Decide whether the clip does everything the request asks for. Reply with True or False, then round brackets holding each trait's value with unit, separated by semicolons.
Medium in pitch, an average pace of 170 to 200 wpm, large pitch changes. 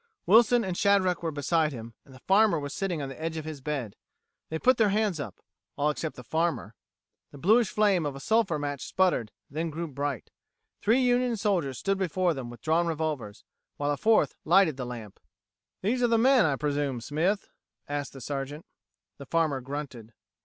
True (155 Hz; 190 wpm; 5.8 semitones)